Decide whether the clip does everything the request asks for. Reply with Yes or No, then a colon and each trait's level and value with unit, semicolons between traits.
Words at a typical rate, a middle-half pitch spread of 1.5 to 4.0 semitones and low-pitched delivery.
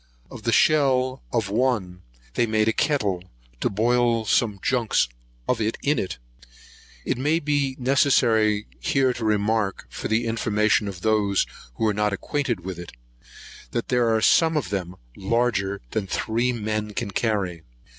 Yes: average, 155 wpm; average, 3.7 semitones; low, 110 Hz